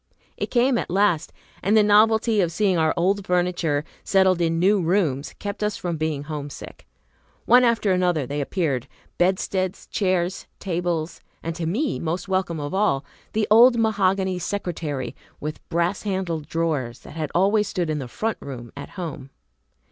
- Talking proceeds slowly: No, average, 165 wpm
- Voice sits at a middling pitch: Yes, medium, 180 Hz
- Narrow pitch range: No, average, 4.3 semitones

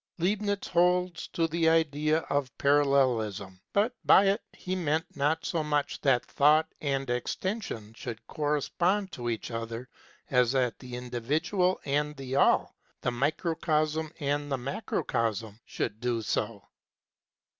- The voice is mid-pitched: Yes, medium, 145 Hz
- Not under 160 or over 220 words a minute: No, slow, 135 wpm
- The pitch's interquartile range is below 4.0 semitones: No, average, 4.9 semitones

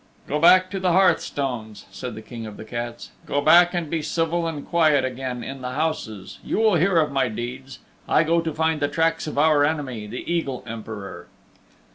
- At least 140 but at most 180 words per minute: No, average, 200 wpm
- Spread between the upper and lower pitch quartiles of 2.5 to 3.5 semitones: No, average, 5.2 semitones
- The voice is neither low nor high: Yes, medium, 145 Hz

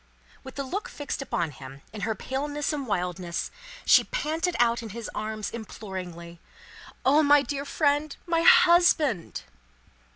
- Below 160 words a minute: Yes, average, 140 wpm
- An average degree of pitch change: No, wide, 7.1 semitones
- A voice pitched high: Yes, very high, 265 Hz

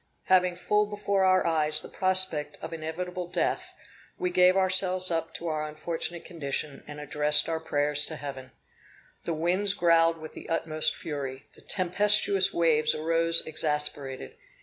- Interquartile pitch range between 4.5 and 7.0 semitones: No, average, 3.3 semitones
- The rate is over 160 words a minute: No, average, 150 wpm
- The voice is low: No, medium, 165 Hz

